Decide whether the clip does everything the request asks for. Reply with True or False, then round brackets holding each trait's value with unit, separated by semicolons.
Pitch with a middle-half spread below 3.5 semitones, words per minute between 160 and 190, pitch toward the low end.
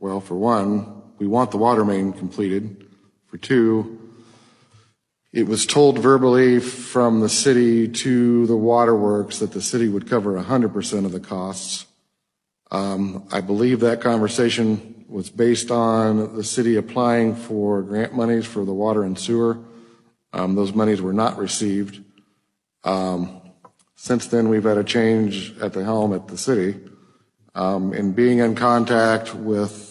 False (2.7 semitones; 150 wpm; 110 Hz)